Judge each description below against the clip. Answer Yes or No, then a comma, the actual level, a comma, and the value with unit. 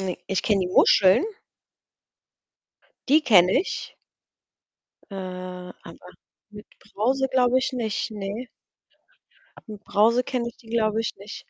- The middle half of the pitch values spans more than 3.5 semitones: Yes, average, 4.3 semitones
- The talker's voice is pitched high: Yes, high, 215 Hz